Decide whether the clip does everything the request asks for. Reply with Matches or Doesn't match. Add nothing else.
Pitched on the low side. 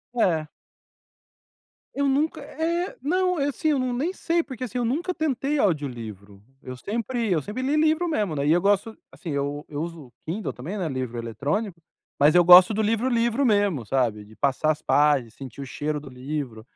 Doesn't match